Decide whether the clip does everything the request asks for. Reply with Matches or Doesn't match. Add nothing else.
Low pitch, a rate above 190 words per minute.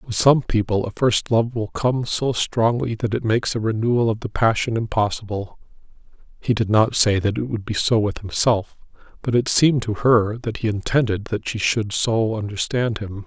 Matches